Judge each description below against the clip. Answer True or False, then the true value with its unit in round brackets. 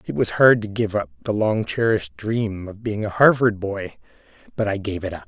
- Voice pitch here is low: True (105 Hz)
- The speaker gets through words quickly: True (225 wpm)